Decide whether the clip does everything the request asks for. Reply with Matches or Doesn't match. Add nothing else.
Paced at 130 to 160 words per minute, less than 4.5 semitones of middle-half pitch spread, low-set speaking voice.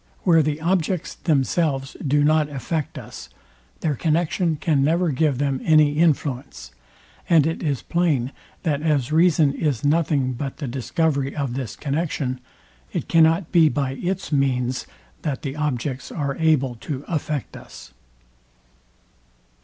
Doesn't match